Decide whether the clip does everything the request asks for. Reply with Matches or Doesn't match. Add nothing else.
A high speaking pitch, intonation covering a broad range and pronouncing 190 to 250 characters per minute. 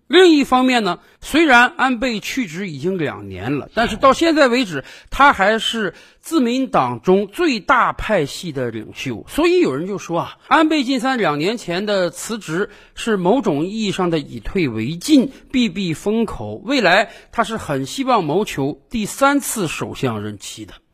Matches